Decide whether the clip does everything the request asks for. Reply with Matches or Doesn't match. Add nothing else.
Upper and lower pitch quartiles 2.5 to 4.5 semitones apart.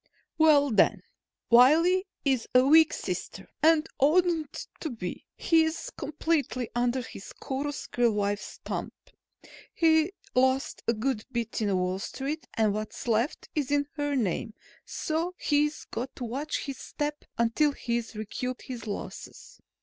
Doesn't match